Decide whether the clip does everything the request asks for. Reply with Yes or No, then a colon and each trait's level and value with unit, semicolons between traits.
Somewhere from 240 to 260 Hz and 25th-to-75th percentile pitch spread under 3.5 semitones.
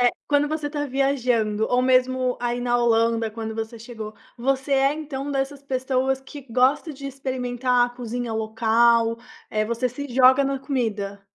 Yes: very high, 250 Hz; average, 2.8 semitones